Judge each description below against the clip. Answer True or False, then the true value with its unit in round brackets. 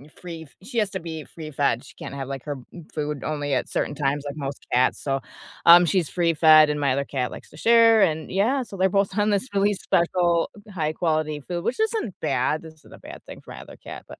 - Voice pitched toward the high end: False (160 Hz)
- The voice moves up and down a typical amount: True (4.5 semitones)